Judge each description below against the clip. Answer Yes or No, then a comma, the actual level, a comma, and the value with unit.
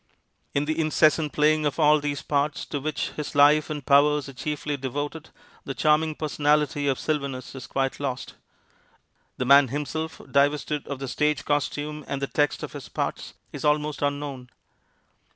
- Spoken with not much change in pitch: Yes, narrow, 1.4 semitones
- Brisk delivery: No, average, 165 wpm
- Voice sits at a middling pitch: Yes, medium, 145 Hz